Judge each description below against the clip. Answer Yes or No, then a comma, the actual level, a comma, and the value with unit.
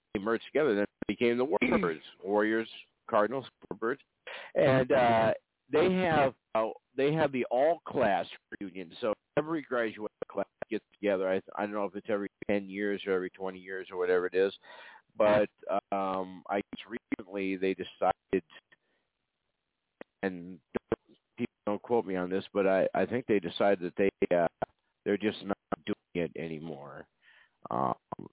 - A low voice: Yes, low, 100 Hz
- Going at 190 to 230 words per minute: No, average, 155 wpm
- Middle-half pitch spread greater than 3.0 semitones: No, average, 2.7 semitones